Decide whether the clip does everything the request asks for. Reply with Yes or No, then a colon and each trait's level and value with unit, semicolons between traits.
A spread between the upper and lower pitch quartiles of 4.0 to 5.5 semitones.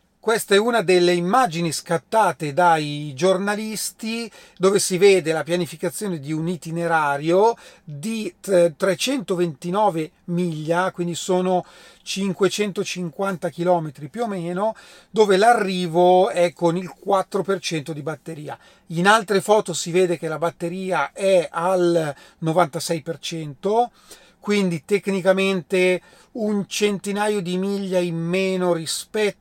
No: average, 2.8 semitones